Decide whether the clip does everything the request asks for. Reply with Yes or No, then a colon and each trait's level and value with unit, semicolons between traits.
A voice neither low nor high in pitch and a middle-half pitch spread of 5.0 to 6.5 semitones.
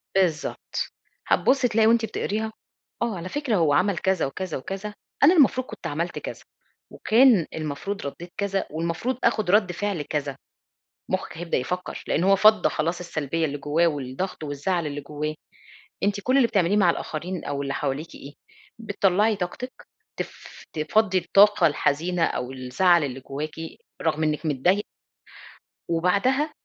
Yes: medium, 175 Hz; wide, 5.4 semitones